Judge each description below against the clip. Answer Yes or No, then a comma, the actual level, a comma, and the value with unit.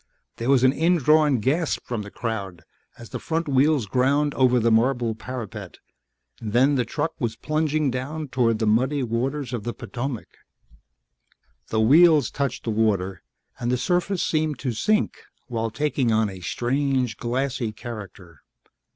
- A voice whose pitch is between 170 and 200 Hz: No, low, 125 Hz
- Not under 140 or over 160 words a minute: Yes, average, 150 wpm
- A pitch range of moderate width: Yes, average, 4.3 semitones